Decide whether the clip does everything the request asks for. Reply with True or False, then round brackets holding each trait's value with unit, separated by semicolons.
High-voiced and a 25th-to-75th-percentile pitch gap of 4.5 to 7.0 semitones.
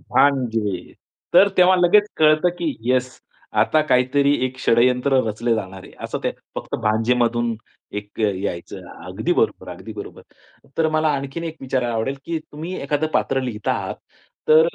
False (130 Hz; 5.1 semitones)